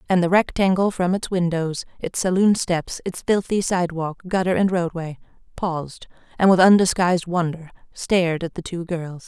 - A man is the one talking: No, female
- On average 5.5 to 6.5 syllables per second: No, 5.1 syllables/s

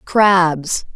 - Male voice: No, female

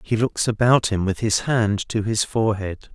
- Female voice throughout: No, male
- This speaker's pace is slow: No, fast, 205 wpm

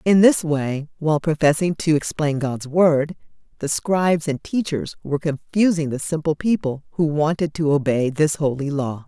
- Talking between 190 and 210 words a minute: No, average, 165 wpm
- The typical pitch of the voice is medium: Yes, medium, 155 Hz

